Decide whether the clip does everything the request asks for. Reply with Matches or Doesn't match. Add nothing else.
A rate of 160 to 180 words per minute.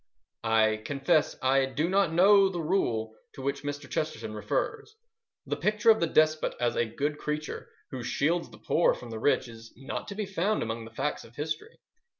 Doesn't match